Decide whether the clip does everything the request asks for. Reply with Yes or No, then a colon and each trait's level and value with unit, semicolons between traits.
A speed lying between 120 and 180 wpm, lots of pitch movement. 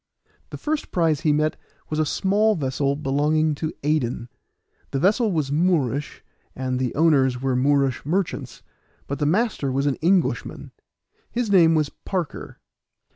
No: average, 145 wpm; average, 4.2 semitones